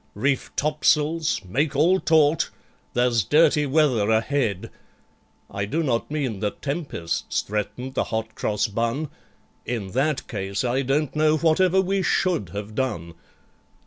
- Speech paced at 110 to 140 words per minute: Yes, slow, 135 wpm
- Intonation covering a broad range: Yes, wide, 6.0 semitones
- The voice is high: No, low, 135 Hz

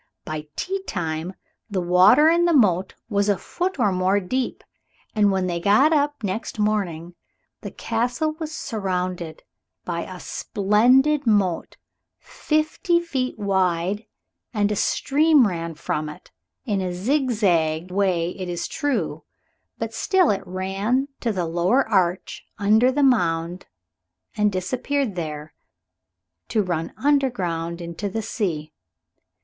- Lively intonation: Yes, wide, 6.4 semitones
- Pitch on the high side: Yes, high, 200 Hz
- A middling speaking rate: No, slow, 130 wpm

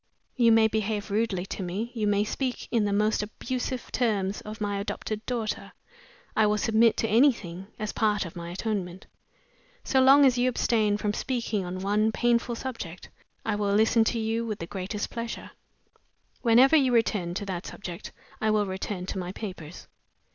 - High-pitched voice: Yes, high, 215 Hz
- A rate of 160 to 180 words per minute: Yes, average, 175 wpm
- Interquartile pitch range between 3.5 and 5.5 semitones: No, average, 2.8 semitones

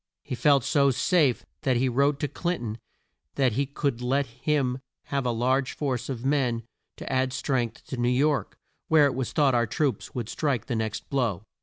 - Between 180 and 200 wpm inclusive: Yes, average, 195 wpm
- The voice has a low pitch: Yes, low, 130 Hz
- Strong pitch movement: No, average, 2.7 semitones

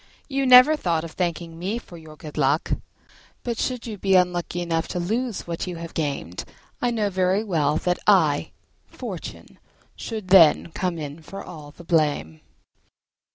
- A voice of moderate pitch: Yes, medium, 175 Hz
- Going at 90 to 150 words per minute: No, average, 165 wpm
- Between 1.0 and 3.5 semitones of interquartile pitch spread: No, average, 4.2 semitones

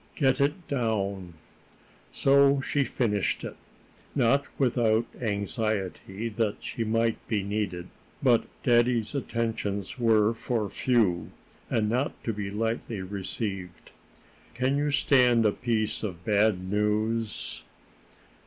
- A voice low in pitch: Yes, low, 110 Hz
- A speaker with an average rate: No, slow, 115 wpm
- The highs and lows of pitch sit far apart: No, average, 3.1 semitones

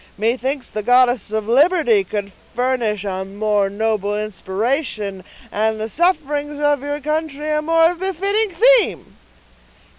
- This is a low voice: No, very high, 250 Hz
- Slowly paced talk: Yes, slow, 125 wpm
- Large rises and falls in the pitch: Yes, wide, 6.3 semitones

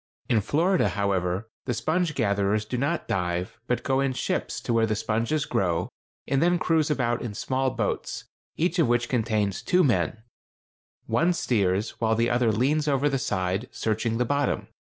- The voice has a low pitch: Yes, low, 120 Hz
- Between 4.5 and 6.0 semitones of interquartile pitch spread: Yes, average, 4.9 semitones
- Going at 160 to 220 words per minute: Yes, average, 170 wpm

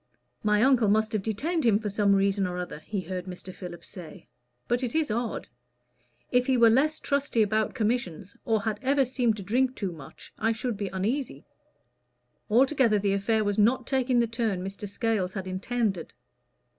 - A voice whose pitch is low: No, high, 220 Hz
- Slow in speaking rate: No, average, 180 wpm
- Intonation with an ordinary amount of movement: Yes, average, 3.8 semitones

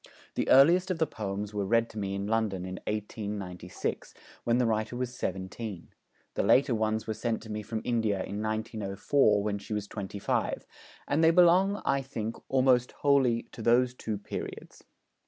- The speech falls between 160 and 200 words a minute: Yes, average, 175 wpm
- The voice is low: Yes, low, 110 Hz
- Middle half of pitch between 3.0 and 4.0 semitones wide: Yes, average, 3.7 semitones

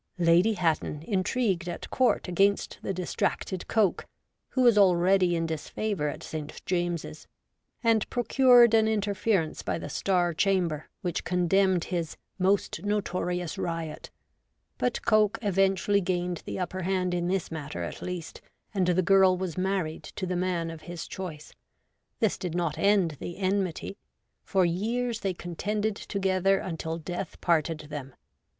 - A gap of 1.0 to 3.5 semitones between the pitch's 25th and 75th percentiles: Yes, average, 2.8 semitones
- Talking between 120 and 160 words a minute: Yes, average, 150 wpm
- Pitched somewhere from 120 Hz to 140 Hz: No, medium, 185 Hz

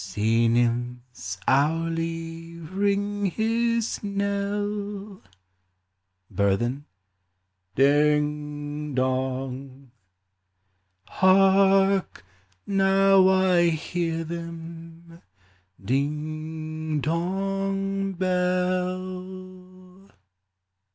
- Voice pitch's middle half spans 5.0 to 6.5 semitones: Yes, wide, 5.5 semitones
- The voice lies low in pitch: No, medium, 165 Hz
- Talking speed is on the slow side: Yes, slow, 55 wpm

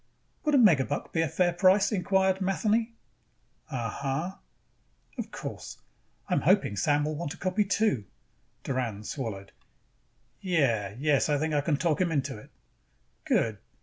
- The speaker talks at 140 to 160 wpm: Yes, average, 150 wpm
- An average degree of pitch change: No, wide, 6.1 semitones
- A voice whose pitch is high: No, medium, 155 Hz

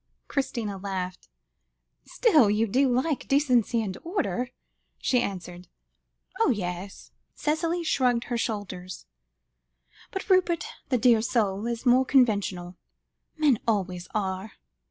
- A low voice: No, high, 230 Hz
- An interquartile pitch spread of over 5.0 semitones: Yes, wide, 5.5 semitones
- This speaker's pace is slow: Yes, slow, 115 wpm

